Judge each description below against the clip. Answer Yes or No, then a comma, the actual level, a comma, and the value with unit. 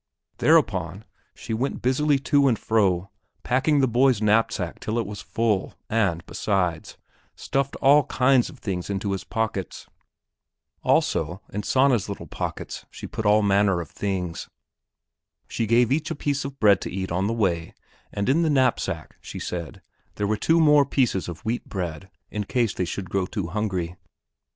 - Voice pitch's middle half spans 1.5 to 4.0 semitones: No, wide, 5.4 semitones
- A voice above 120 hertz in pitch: No, low, 105 Hz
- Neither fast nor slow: Yes, average, 170 wpm